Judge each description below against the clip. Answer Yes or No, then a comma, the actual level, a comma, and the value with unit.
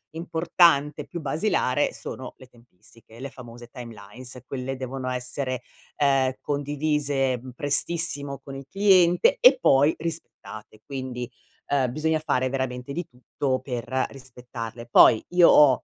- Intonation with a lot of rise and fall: No, average, 2.9 semitones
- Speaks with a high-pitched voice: No, low, 135 Hz